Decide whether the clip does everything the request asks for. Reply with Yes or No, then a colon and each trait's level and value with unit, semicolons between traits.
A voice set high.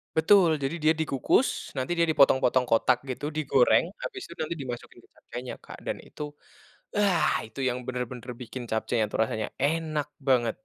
No: low, 135 Hz